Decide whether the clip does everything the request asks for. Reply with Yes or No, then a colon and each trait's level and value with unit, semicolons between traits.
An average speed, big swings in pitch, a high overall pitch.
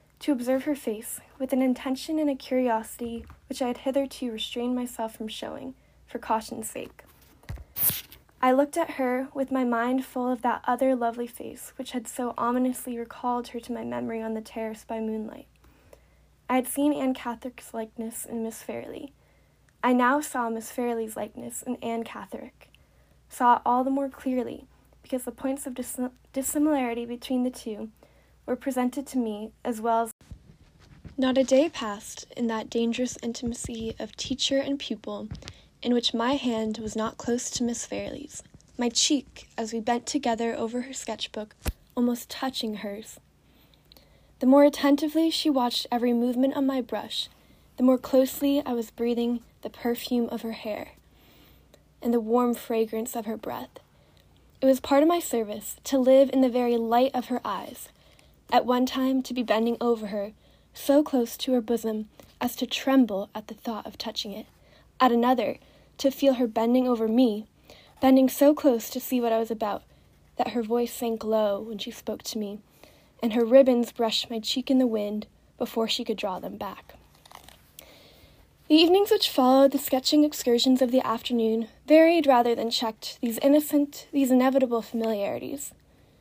No: average, 175 wpm; narrow, 2.5 semitones; high, 245 Hz